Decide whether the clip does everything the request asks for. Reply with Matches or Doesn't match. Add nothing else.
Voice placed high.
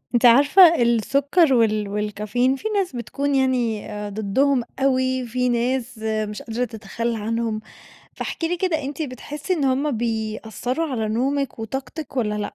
Matches